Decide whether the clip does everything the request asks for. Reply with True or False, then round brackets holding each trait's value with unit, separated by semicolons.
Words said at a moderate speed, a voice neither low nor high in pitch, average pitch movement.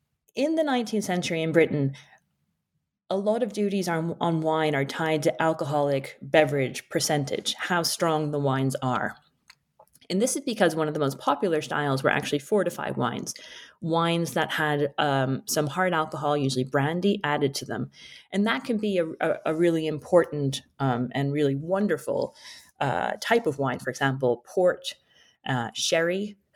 True (165 wpm; 160 Hz; 4.7 semitones)